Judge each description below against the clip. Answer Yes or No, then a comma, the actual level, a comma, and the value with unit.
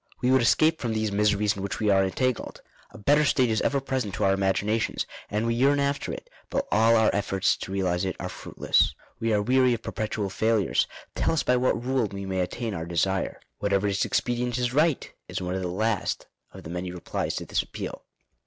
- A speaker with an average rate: No, fast, 220 wpm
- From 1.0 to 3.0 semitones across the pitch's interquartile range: No, average, 4.2 semitones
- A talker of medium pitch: No, low, 110 Hz